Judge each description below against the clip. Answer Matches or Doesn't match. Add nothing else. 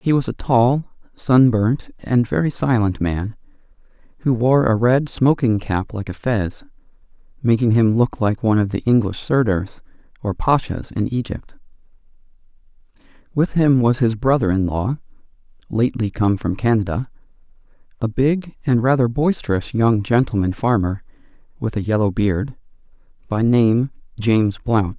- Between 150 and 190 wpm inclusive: Doesn't match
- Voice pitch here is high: Doesn't match